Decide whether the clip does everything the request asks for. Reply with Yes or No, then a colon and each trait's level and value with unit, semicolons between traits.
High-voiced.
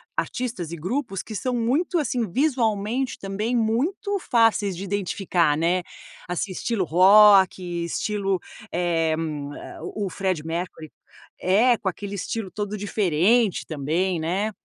Yes: high, 200 Hz